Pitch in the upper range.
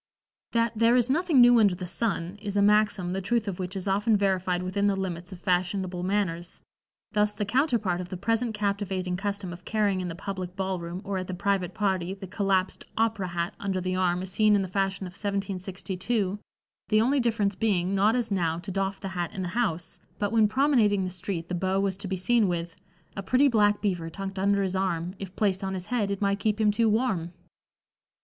Yes: high, 195 Hz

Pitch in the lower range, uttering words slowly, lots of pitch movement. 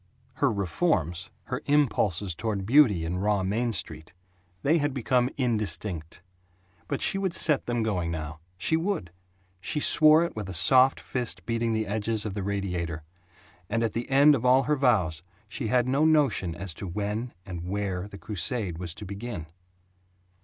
No: low, 105 Hz; average, 165 wpm; wide, 5.8 semitones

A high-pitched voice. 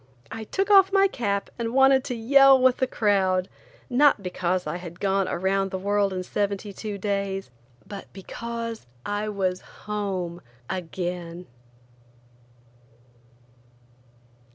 Yes: high, 200 Hz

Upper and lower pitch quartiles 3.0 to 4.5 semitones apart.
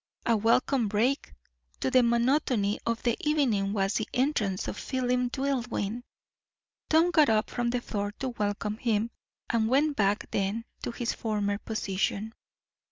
Yes: average, 3.5 semitones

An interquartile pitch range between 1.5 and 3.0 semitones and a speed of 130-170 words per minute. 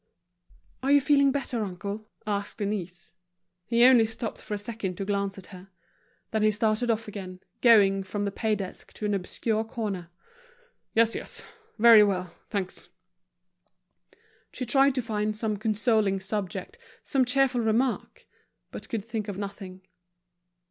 Yes: average, 2.7 semitones; average, 150 wpm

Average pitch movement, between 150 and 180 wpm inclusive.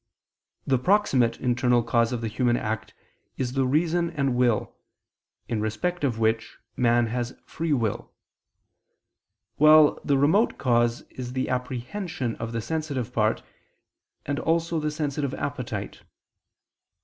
No: average, 4.3 semitones; slow, 135 wpm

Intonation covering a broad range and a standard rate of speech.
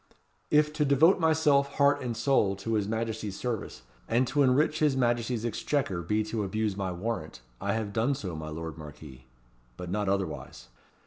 Yes: wide, 6.1 semitones; average, 175 wpm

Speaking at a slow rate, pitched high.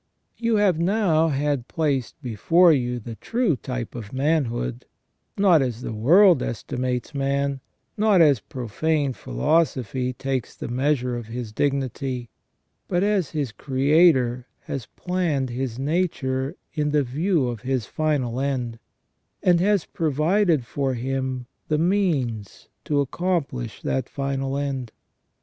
No: slow, 130 wpm; low, 135 Hz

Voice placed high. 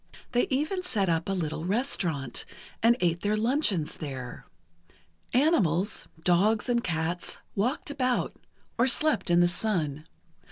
Yes: high, 195 Hz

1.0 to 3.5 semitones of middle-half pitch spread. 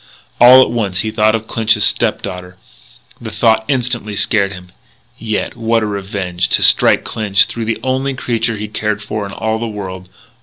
Yes: narrow, 2.4 semitones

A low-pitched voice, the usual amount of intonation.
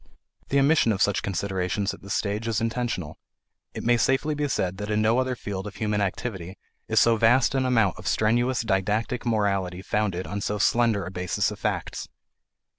Yes: low, 105 Hz; average, 3.7 semitones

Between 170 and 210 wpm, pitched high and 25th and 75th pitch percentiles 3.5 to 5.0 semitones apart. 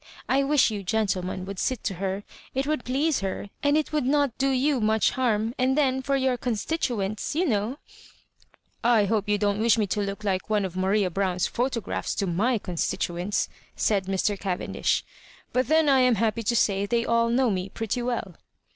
Yes: average, 200 wpm; high, 220 Hz; average, 4.7 semitones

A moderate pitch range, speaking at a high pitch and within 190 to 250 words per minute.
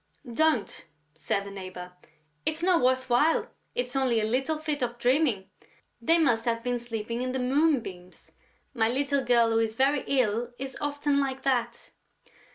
No: average, 3.5 semitones; very high, 250 Hz; average, 165 wpm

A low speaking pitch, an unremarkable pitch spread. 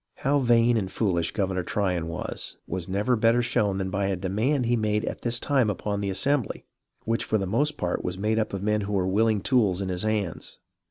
Yes: low, 105 Hz; average, 3.5 semitones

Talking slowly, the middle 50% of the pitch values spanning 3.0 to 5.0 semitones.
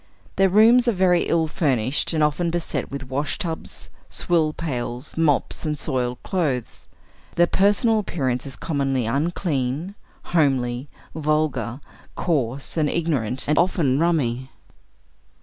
Yes: slow, 125 wpm; average, 4.6 semitones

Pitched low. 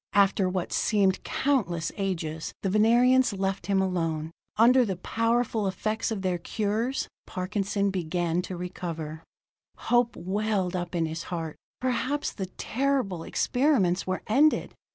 No: high, 195 Hz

